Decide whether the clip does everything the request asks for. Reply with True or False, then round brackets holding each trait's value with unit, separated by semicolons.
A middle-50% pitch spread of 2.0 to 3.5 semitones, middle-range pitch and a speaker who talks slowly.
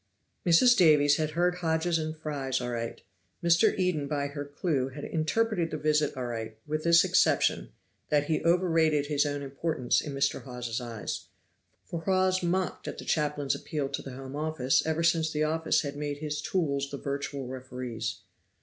False (3.0 semitones; 150 Hz; 170 wpm)